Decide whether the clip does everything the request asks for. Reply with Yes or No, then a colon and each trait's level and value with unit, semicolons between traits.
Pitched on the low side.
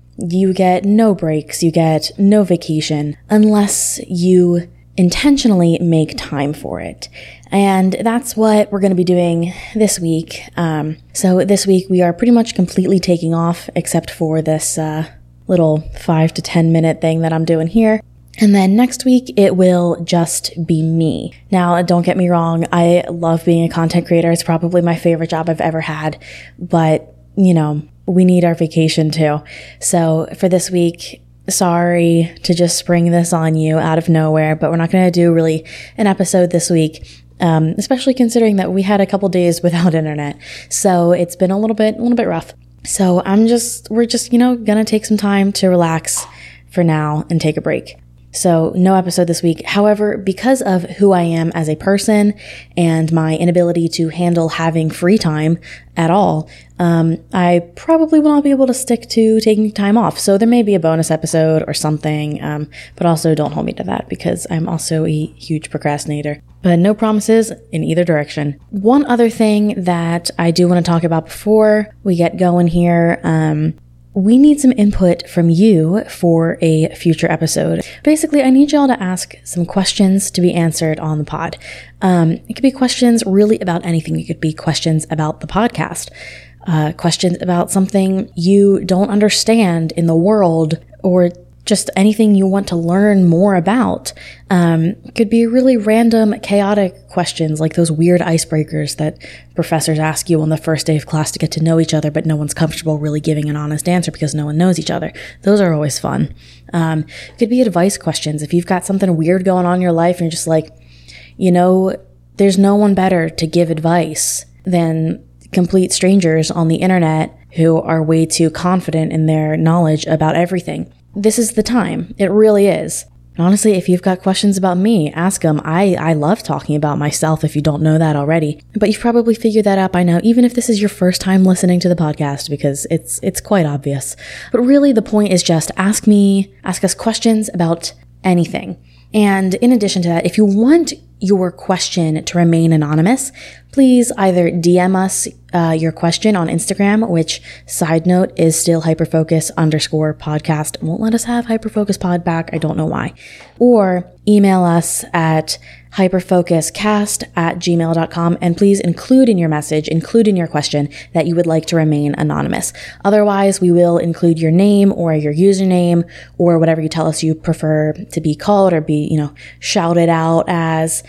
No: medium, 170 Hz